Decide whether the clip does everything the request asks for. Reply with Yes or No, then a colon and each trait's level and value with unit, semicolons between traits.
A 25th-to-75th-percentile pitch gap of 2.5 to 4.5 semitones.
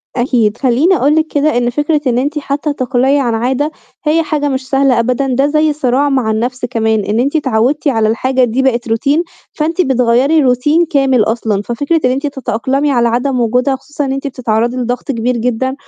Yes: average, 3.2 semitones